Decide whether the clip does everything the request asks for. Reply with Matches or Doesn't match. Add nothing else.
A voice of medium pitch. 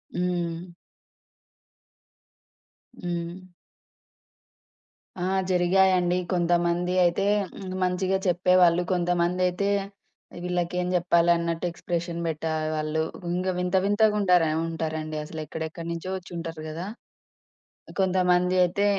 Matches